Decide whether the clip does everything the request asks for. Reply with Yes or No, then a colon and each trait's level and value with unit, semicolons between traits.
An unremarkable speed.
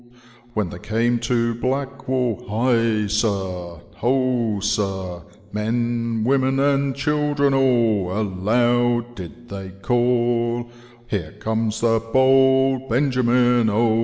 No: slow, 115 wpm